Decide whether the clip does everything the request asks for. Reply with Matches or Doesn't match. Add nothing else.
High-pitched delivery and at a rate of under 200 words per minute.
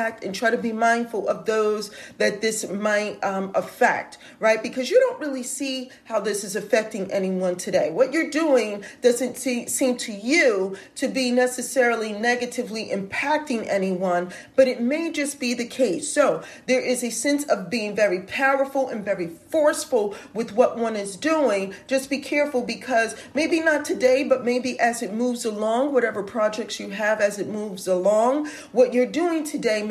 Matches